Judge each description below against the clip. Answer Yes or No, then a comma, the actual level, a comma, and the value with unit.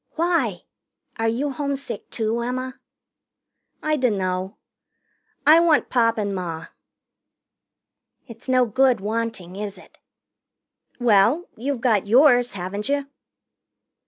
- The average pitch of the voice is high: Yes, high, 235 Hz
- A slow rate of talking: Yes, slow, 105 wpm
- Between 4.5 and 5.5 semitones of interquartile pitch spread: Yes, average, 4.9 semitones